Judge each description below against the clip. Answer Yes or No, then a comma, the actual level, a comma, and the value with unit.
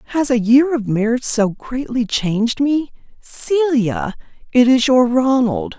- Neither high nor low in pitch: No, very high, 250 Hz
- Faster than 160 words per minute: No, average, 145 wpm